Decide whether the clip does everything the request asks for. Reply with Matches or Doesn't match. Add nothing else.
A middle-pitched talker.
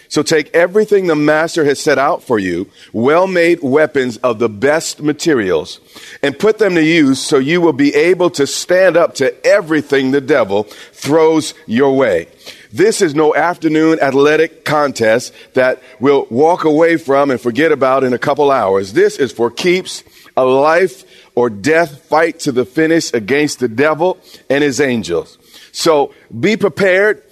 Matches